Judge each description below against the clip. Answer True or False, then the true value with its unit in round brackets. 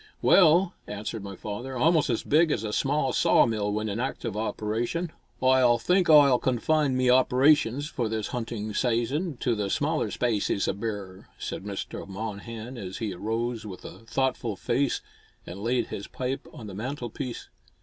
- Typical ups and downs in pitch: True (4.0 semitones)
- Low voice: True (120 Hz)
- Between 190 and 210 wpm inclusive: False (165 wpm)